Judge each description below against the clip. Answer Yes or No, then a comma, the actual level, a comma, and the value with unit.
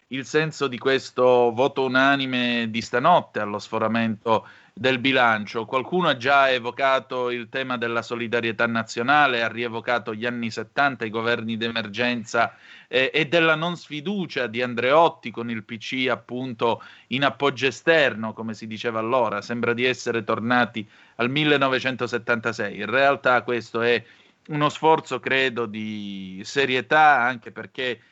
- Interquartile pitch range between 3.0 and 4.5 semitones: No, narrow, 2.6 semitones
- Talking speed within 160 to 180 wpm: No, average, 135 wpm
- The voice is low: Yes, low, 120 Hz